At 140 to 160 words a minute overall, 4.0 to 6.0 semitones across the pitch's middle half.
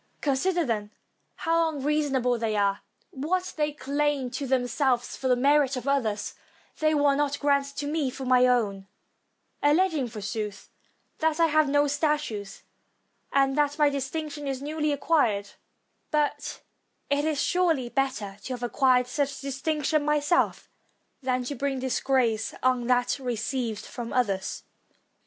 No: average, 145 wpm; average, 3.1 semitones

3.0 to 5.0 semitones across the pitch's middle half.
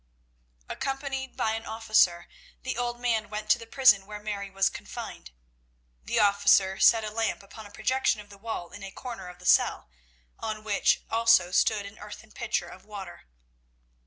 No: narrow, 2.5 semitones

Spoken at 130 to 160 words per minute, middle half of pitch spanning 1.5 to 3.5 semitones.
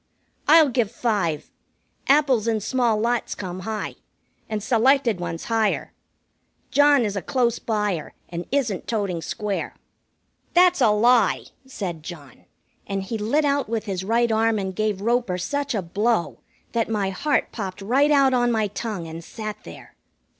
No: average, 155 wpm; average, 3.9 semitones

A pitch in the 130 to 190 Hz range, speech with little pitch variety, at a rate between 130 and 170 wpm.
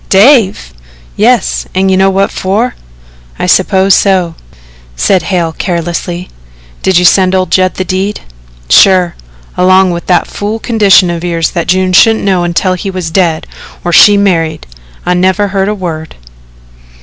Yes: medium, 185 Hz; narrow, 2.0 semitones; average, 155 wpm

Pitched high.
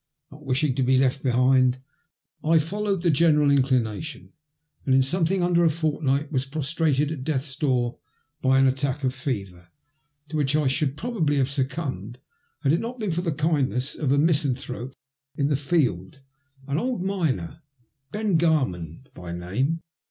No: medium, 140 Hz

